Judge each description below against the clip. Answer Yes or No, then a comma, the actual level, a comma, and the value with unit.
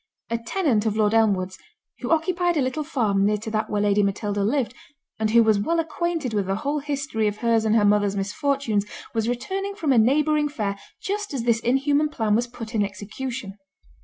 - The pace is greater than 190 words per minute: Yes, average, 200 wpm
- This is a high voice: Yes, high, 230 Hz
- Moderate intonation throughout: No, wide, 5.7 semitones